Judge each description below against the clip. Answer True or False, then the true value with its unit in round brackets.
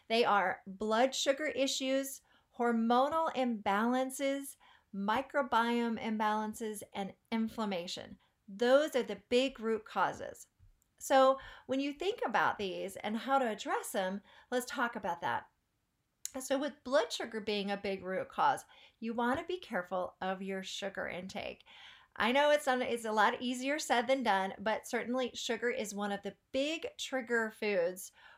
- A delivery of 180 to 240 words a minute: False (145 wpm)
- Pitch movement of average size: True (4.5 semitones)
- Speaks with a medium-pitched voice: False (235 Hz)